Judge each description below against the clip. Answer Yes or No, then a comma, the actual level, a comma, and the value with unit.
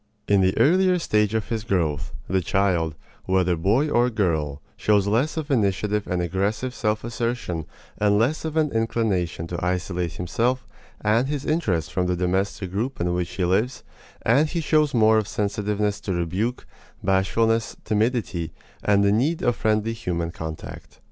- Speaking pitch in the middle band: No, low, 105 Hz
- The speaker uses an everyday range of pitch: Yes, average, 4.6 semitones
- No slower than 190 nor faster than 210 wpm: No, average, 160 wpm